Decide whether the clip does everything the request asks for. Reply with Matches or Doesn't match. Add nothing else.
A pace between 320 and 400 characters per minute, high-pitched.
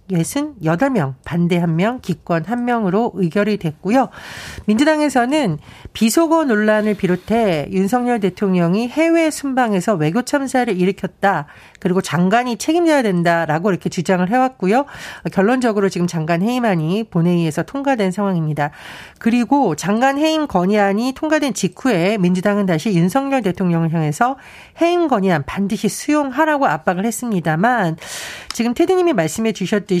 Matches